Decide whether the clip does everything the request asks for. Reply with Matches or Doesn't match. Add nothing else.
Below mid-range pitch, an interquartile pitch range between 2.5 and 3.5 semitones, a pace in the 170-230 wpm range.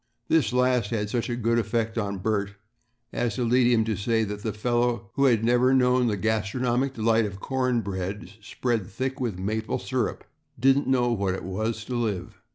Matches